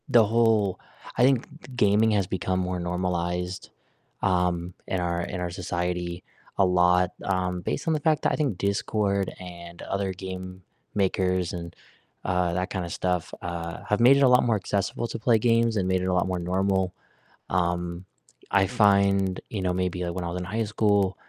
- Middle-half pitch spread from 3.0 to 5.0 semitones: No, narrow, 2.4 semitones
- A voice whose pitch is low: Yes, very low, 95 Hz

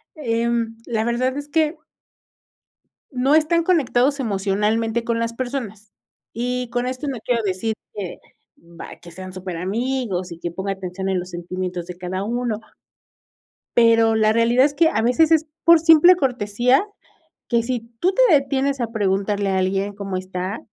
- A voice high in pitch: Yes, high, 230 Hz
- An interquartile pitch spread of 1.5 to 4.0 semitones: No, average, 5.2 semitones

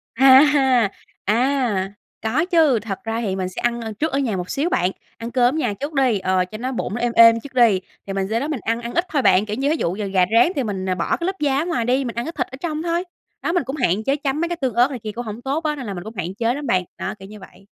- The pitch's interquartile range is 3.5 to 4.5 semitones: No, average, 5.0 semitones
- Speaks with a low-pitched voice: No, high, 240 Hz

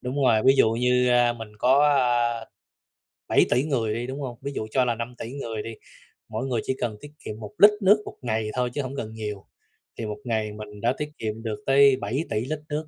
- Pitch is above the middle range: No, low, 120 Hz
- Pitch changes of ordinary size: Yes, average, 3.3 semitones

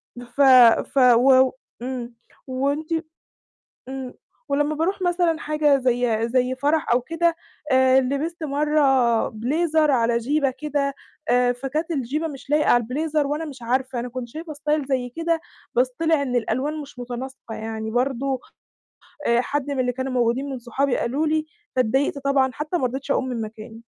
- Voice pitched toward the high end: Yes, very high, 265 Hz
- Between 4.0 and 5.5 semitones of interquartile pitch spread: No, average, 3.3 semitones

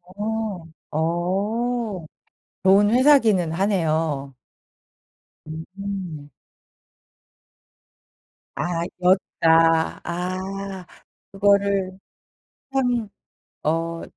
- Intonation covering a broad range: No, average, 3.6 semitones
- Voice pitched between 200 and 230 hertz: No, high, 190 Hz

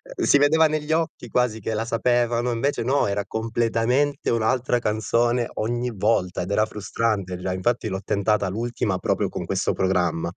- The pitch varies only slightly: No, average, 3.3 semitones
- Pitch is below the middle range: Yes, low, 115 Hz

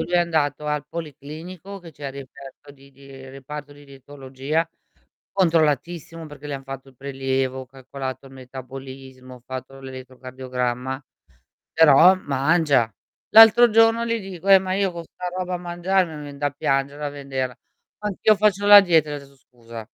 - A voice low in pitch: No, medium, 145 Hz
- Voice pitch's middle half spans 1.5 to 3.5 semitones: No, average, 4.5 semitones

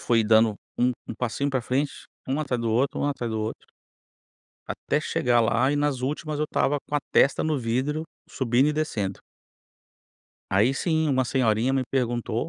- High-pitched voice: No, low, 130 Hz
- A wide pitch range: No, average, 3.8 semitones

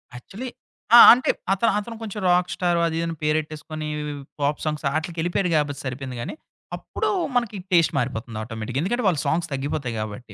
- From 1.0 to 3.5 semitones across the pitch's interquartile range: No, average, 5.1 semitones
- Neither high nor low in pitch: Yes, medium, 155 Hz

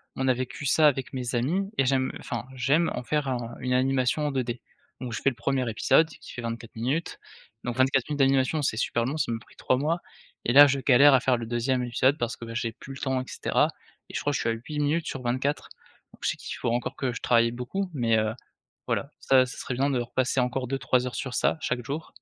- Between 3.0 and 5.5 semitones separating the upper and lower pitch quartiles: No, narrow, 2.4 semitones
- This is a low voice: Yes, low, 130 Hz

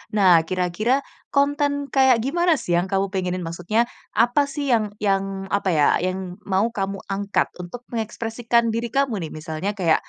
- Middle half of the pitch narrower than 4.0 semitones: No, average, 4.7 semitones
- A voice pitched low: No, high, 205 Hz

